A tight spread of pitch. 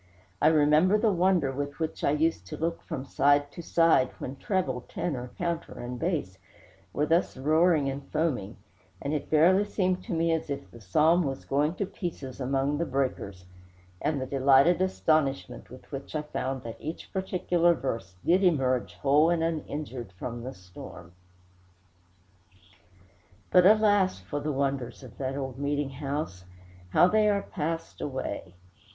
No: average, 4.3 semitones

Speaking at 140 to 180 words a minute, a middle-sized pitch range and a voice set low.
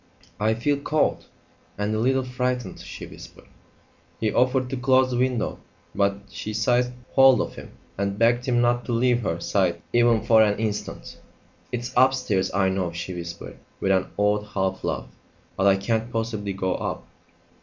Yes: average, 170 wpm; average, 3.9 semitones; low, 110 Hz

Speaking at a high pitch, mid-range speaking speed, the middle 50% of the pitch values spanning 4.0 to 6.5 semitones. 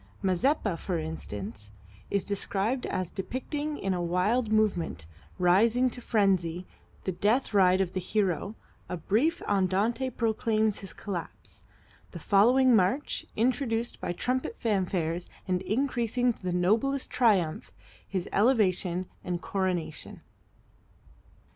No: high, 200 Hz; slow, 120 wpm; average, 4.6 semitones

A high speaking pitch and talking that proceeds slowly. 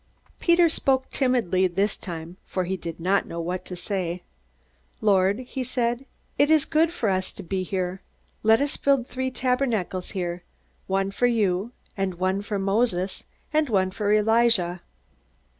No: high, 200 Hz; average, 160 wpm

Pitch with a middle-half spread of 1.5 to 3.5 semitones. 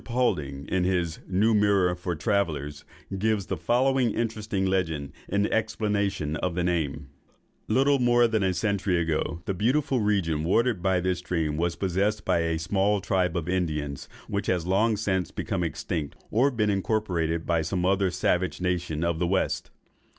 No: average, 3.9 semitones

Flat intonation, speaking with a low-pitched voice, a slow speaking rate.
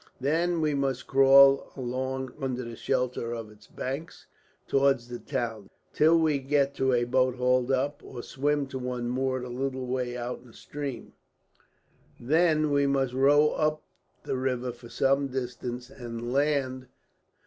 No: narrow, 2.1 semitones; low, 130 Hz; average, 160 wpm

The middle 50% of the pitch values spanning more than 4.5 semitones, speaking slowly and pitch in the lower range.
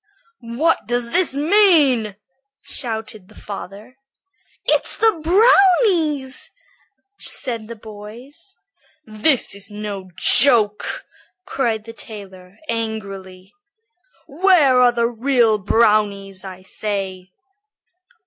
No: average, 5.2 semitones; slow, 90 wpm; high, 230 Hz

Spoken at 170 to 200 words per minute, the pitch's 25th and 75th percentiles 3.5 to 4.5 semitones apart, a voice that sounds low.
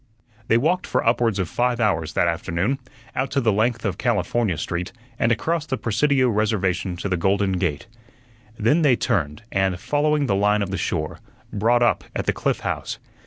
No: average, 180 wpm; average, 4.9 semitones; low, 105 Hz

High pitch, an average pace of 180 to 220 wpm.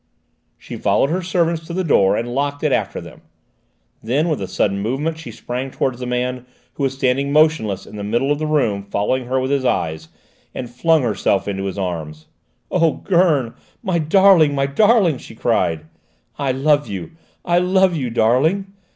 No: low, 135 Hz; average, 185 wpm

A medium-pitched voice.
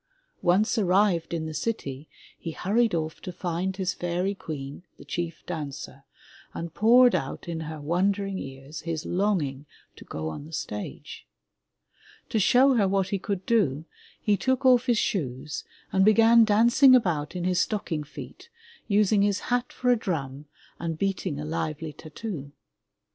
Yes: medium, 180 Hz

